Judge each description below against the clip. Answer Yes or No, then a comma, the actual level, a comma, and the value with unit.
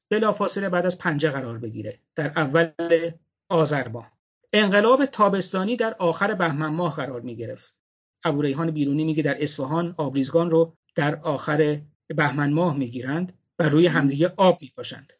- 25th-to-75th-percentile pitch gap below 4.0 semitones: Yes, average, 3.4 semitones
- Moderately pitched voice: Yes, medium, 160 Hz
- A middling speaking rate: Yes, average, 135 wpm